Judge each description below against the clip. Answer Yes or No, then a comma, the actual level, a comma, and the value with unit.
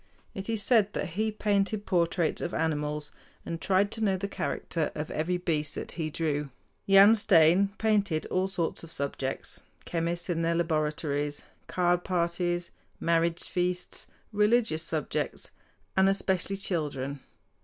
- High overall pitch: No, medium, 175 Hz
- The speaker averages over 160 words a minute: No, average, 140 wpm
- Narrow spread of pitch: No, average, 3.6 semitones